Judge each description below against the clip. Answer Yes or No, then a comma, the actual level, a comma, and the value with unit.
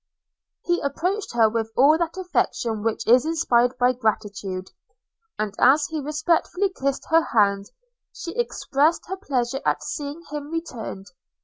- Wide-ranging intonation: Yes, wide, 6.4 semitones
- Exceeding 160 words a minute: No, average, 140 wpm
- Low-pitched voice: No, very high, 275 Hz